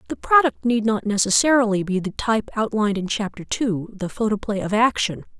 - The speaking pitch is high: Yes, high, 215 Hz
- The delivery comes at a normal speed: Yes, average, 180 wpm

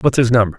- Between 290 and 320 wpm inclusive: Yes, fast, 305 wpm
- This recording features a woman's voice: No, male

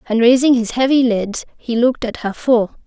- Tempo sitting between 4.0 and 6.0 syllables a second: Yes, 5.2 syllables/s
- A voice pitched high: Yes, high, 240 Hz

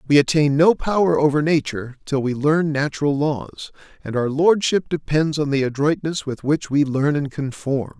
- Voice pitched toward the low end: No, medium, 145 Hz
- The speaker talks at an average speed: Yes, average, 180 wpm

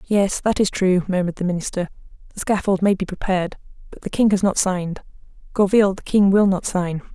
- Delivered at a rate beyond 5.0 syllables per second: Yes, 6.0 syllables/s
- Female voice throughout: Yes, female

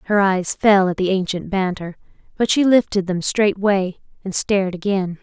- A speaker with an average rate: Yes, average, 170 wpm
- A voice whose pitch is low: No, high, 195 Hz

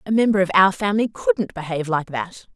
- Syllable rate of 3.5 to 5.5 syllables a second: No, 6.0 syllables/s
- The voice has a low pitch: No, medium, 185 Hz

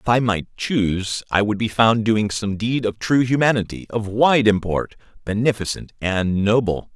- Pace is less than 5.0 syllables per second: Yes, 4.5 syllables/s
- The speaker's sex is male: Yes, male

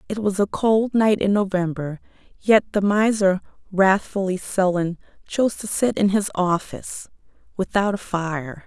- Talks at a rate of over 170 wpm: No, average, 145 wpm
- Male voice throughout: No, female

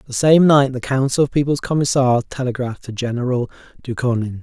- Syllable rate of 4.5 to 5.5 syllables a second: No, 5.9 syllables/s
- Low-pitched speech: Yes, low, 130 Hz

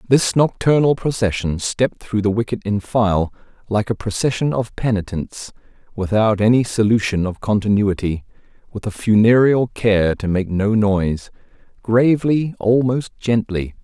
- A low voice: Yes, low, 110 Hz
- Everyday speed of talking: No, slow, 125 wpm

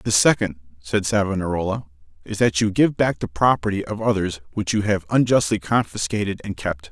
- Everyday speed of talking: Yes, average, 175 wpm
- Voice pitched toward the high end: No, low, 100 Hz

